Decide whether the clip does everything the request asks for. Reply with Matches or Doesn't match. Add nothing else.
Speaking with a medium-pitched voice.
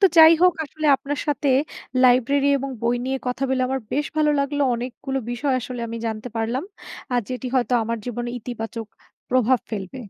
Doesn't match